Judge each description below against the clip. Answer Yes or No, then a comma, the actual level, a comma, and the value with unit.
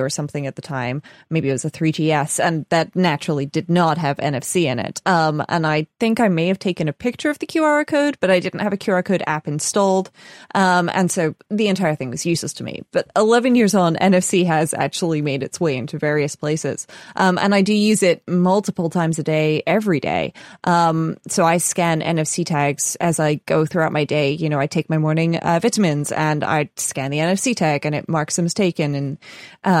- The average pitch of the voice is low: No, medium, 165 Hz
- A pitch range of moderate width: Yes, average, 3.6 semitones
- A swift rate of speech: Yes, fast, 225 wpm